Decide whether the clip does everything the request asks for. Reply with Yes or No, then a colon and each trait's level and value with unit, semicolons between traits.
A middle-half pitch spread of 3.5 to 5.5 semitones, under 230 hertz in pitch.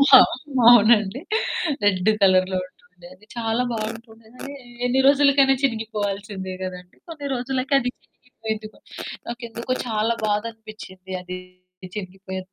Yes: average, 4.2 semitones; high, 220 Hz